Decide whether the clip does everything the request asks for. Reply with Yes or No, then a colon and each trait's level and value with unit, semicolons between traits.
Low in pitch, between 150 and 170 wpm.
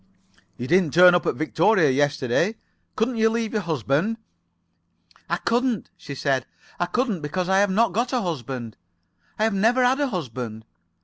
No: medium, 180 Hz; average, 165 wpm